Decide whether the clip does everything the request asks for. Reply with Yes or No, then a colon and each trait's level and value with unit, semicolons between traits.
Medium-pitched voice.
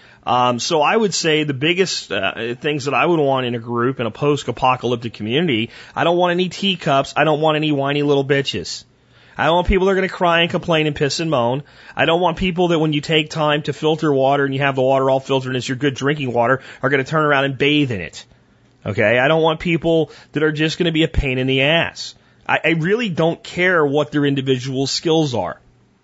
Yes: medium, 145 Hz